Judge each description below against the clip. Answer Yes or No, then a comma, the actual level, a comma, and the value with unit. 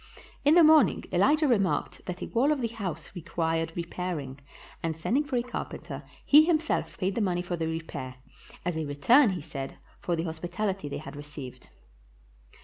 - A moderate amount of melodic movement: No, wide, 6.8 semitones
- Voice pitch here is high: No, medium, 175 Hz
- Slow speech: No, average, 180 wpm